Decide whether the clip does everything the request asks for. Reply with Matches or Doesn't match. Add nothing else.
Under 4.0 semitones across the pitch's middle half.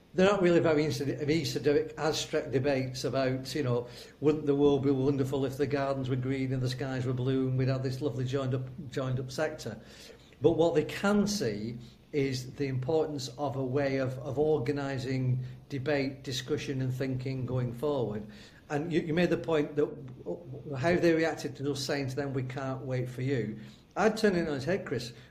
Matches